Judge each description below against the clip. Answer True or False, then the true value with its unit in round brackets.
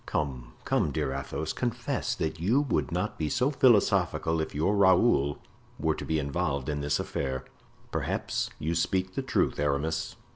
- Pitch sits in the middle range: False (80 Hz)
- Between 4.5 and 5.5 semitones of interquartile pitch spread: True (4.8 semitones)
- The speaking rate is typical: True (160 wpm)